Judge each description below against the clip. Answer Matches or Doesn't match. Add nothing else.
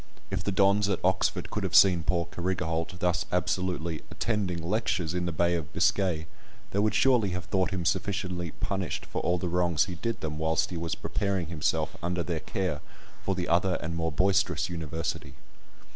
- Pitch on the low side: Matches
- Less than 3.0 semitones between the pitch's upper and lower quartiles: Matches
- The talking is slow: Doesn't match